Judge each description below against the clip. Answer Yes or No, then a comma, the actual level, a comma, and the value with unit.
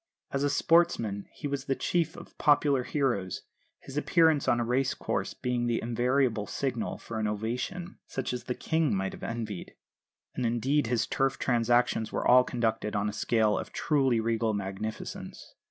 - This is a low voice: Yes, low, 120 Hz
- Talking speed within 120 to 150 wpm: No, average, 170 wpm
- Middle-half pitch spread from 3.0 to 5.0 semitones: Yes, average, 3.7 semitones